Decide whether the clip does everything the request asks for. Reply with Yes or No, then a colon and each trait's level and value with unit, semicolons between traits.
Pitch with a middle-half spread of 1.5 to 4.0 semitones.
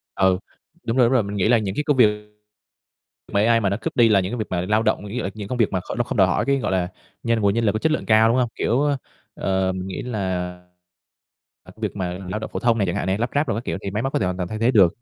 Yes: average, 3.6 semitones